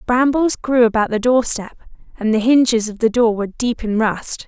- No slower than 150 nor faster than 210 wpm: Yes, average, 200 wpm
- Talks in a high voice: Yes, high, 230 Hz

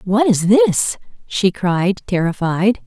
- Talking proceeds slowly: Yes, slow, 125 wpm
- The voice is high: Yes, high, 200 Hz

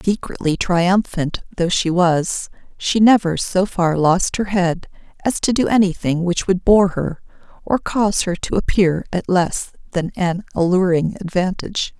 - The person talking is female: Yes, female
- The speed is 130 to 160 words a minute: Yes, average, 155 wpm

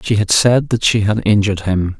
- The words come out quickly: Yes, fast, 240 wpm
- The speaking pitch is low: Yes, low, 105 Hz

